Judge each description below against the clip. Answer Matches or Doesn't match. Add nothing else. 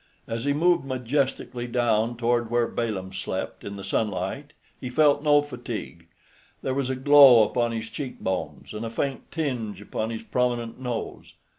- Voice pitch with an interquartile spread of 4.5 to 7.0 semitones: Doesn't match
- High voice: Doesn't match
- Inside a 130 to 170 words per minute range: Matches